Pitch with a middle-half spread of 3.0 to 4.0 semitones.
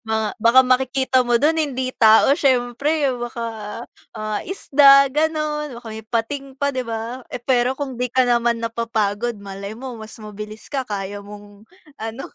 Yes: average, 3.5 semitones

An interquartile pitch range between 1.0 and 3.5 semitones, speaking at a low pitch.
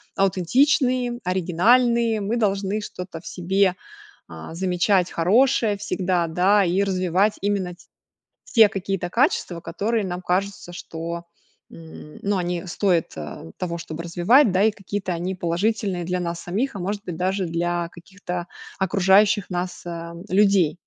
No: average, 2.8 semitones; medium, 185 Hz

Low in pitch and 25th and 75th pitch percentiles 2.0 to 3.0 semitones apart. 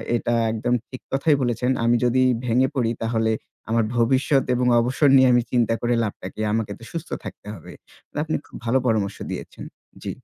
Yes: low, 120 Hz; narrow, 2.4 semitones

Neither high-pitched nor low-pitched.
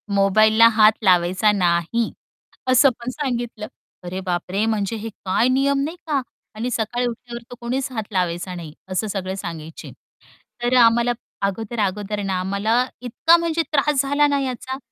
No: high, 220 Hz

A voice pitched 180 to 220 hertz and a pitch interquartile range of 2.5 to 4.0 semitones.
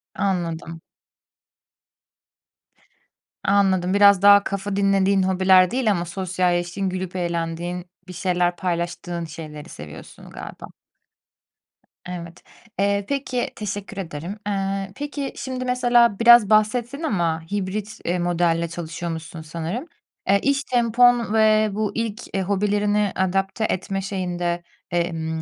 Yes: high, 190 Hz; average, 3.3 semitones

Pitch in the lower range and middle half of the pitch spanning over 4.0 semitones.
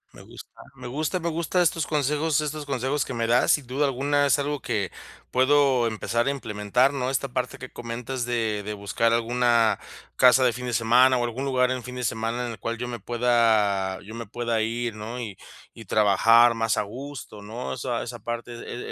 No: low, 120 Hz; narrow, 2.6 semitones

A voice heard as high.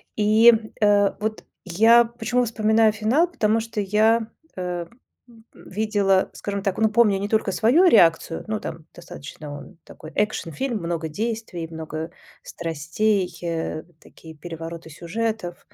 Yes: high, 205 Hz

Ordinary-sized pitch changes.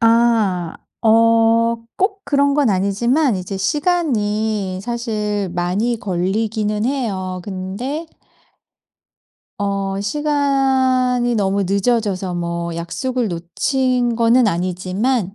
Yes: average, 4.6 semitones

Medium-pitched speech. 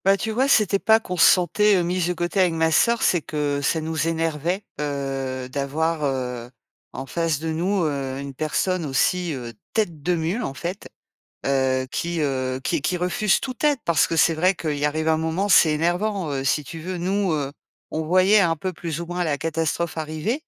Yes: medium, 165 Hz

